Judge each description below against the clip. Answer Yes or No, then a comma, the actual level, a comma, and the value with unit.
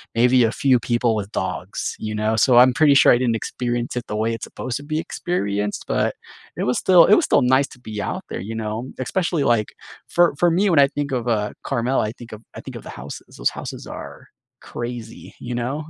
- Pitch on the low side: Yes, low, 120 Hz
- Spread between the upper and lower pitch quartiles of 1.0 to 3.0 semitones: No, average, 3.8 semitones